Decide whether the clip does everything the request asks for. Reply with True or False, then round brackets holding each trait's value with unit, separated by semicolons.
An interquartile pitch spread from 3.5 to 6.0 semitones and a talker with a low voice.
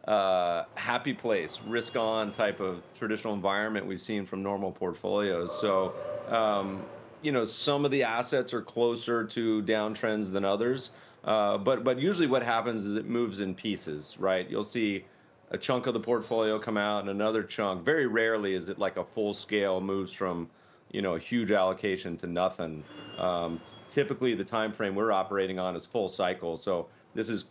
False (3.1 semitones; 105 Hz)